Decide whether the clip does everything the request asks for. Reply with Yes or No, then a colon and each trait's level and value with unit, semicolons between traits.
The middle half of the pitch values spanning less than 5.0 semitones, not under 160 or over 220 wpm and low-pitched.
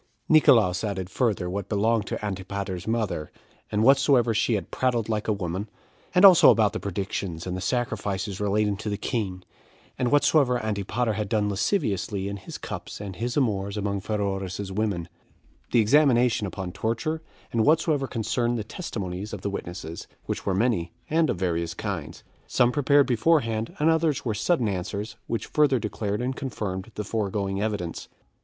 Yes: average, 3.8 semitones; average, 165 wpm; low, 105 Hz